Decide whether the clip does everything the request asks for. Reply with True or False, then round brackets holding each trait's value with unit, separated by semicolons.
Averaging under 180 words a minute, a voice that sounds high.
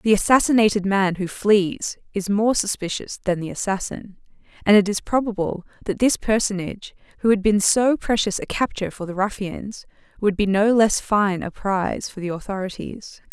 True (170 wpm; 205 Hz)